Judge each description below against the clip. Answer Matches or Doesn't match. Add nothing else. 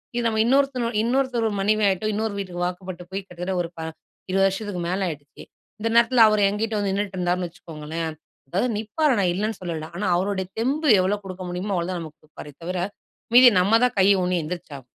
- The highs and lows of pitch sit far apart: Doesn't match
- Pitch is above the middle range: Matches